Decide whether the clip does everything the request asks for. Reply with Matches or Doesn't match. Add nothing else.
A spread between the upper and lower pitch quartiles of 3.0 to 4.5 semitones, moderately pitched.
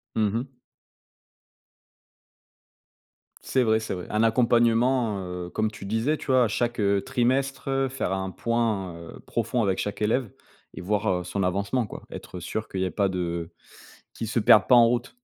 Doesn't match